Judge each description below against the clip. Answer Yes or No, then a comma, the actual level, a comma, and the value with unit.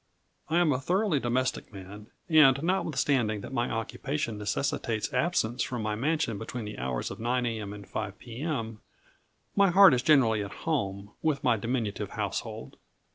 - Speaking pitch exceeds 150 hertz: No, low, 120 Hz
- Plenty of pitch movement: Yes, wide, 5.7 semitones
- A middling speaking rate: Yes, average, 160 wpm